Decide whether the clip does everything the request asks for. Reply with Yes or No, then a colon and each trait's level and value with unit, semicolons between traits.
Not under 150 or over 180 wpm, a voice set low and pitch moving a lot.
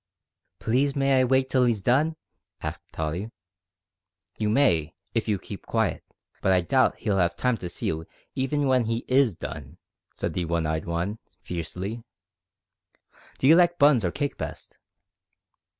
Yes: average, 160 wpm; low, 110 Hz; wide, 7.1 semitones